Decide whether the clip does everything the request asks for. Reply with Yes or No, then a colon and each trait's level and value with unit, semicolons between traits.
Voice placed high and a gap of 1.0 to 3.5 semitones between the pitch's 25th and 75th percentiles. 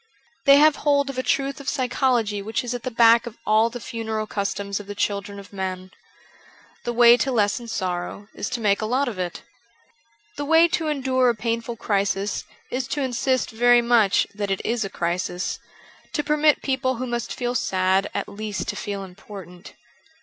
No: high, 230 Hz; average, 4.3 semitones